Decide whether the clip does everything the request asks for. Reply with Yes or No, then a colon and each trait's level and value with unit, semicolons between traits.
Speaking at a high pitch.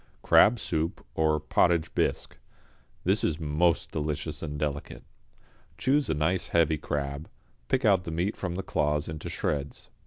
No: very low, 80 Hz